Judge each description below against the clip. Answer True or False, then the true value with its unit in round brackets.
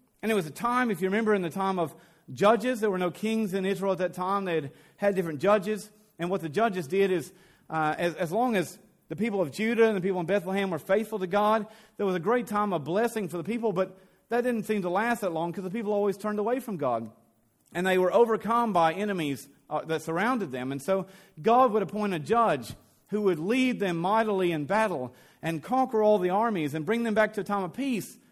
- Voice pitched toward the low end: False (195 Hz)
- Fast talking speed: True (245 wpm)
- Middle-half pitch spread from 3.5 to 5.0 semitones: True (3.8 semitones)